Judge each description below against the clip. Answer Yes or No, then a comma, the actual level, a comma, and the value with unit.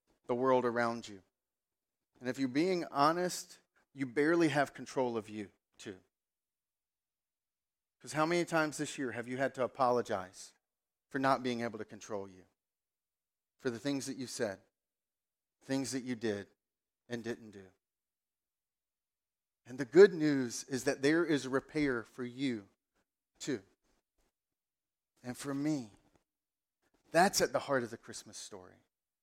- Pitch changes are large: No, average, 3.3 semitones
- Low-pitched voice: Yes, low, 130 Hz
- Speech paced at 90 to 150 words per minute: Yes, average, 145 wpm